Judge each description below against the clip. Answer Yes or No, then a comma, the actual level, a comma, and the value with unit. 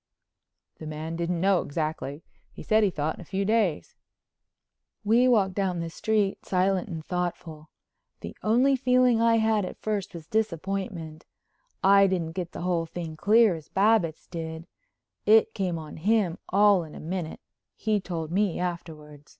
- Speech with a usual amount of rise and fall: Yes, average, 4.3 semitones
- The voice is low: No, medium, 180 Hz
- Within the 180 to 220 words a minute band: No, average, 160 wpm